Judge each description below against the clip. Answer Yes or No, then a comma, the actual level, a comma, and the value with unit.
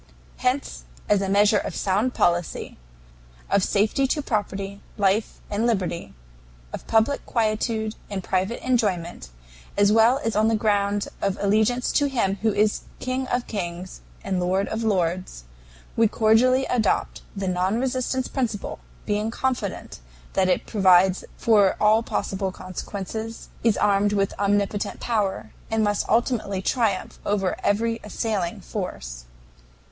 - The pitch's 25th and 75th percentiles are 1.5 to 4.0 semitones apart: Yes, average, 2.8 semitones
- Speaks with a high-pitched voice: Yes, high, 205 Hz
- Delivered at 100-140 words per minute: Yes, slow, 135 wpm